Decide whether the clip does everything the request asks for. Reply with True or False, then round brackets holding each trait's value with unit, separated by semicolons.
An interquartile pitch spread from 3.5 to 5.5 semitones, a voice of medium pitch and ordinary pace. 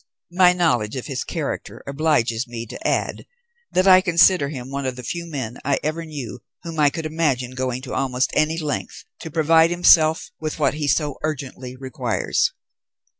True (4.0 semitones; 150 Hz; 175 wpm)